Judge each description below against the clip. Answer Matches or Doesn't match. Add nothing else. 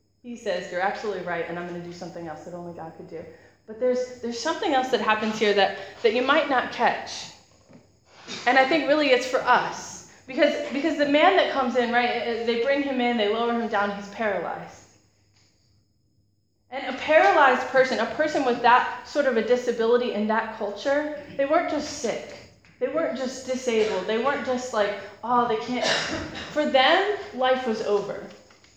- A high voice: Matches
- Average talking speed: Matches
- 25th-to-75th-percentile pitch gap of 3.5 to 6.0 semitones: Matches